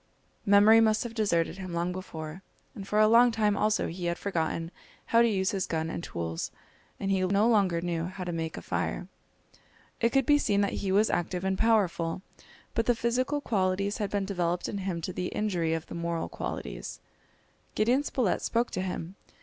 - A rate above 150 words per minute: Yes, average, 200 wpm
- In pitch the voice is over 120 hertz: Yes, high, 190 Hz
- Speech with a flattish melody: No, average, 4.0 semitones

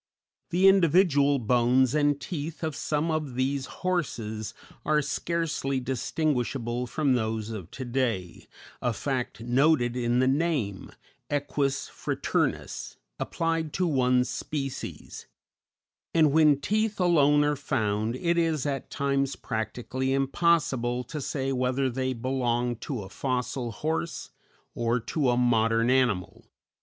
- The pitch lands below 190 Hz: Yes, low, 135 Hz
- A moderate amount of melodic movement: Yes, average, 3.8 semitones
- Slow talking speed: Yes, slow, 125 wpm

